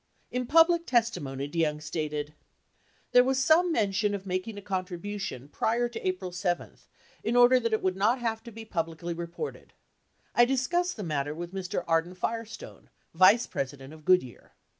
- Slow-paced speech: No, average, 165 wpm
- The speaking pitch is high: Yes, high, 195 Hz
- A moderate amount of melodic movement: No, wide, 6.3 semitones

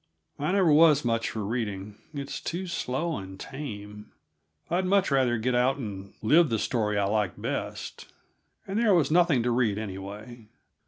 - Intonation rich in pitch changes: Yes, wide, 6.6 semitones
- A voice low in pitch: Yes, low, 120 Hz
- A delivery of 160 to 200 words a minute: Yes, average, 165 wpm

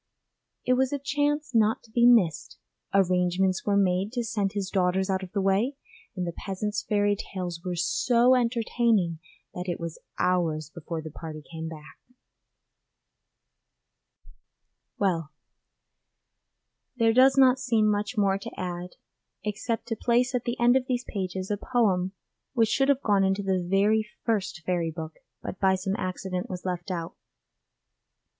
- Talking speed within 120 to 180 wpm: Yes, average, 155 wpm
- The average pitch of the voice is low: No, high, 195 Hz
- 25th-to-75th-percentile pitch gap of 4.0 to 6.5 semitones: Yes, average, 4.4 semitones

